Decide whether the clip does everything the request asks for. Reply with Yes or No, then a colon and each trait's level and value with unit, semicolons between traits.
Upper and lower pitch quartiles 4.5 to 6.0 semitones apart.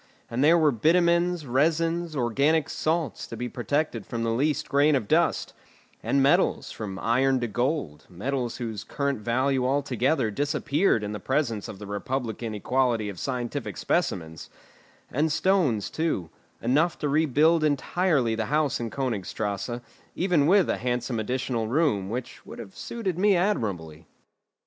Yes: wide, 5.4 semitones